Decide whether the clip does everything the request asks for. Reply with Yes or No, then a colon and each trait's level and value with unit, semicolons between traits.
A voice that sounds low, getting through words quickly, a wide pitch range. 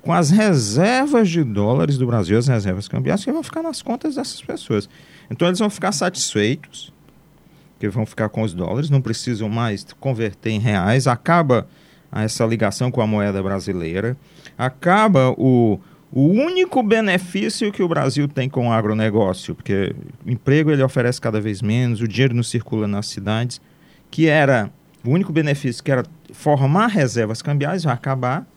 No: low, 130 Hz; average, 165 wpm; wide, 7.4 semitones